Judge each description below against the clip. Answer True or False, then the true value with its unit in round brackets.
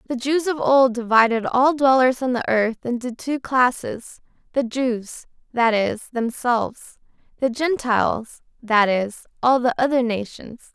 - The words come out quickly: False (135 wpm)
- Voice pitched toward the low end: False (245 Hz)